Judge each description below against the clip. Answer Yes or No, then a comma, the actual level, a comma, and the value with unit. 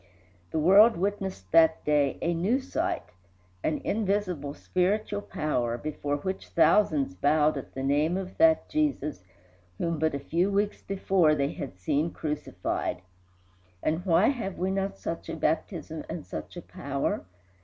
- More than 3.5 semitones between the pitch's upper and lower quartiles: Yes, average, 4.9 semitones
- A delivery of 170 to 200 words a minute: No, average, 150 wpm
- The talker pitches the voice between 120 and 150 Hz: No, medium, 165 Hz